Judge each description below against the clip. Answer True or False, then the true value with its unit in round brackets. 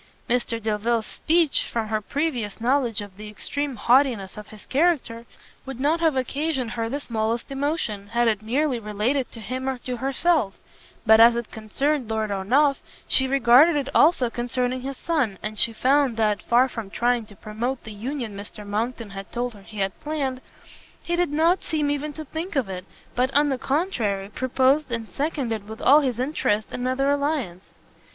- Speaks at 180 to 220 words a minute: True (185 wpm)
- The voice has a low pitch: False (245 Hz)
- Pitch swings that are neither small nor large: True (4.6 semitones)